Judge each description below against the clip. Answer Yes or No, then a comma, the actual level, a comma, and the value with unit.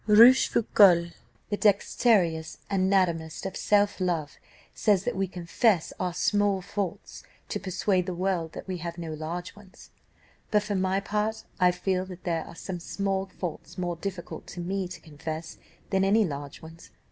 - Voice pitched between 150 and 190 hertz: Yes, medium, 185 Hz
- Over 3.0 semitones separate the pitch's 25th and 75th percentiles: No, average, 2.7 semitones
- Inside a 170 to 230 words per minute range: No, average, 160 wpm